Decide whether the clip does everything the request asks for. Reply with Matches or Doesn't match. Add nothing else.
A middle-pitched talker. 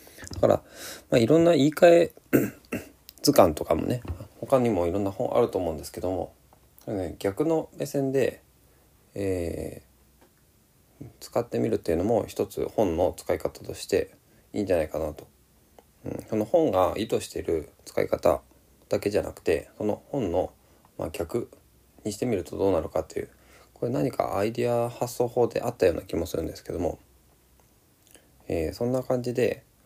Doesn't match